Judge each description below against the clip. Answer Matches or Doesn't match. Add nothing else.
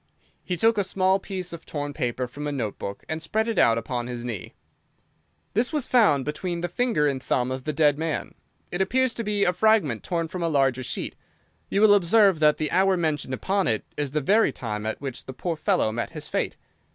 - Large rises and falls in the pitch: Matches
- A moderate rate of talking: Doesn't match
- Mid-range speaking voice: Matches